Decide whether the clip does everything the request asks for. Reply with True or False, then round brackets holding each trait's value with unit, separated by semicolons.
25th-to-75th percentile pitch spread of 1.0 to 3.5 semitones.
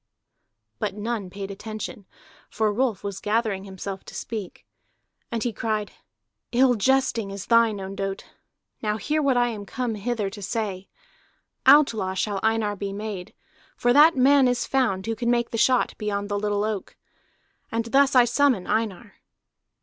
True (3.2 semitones)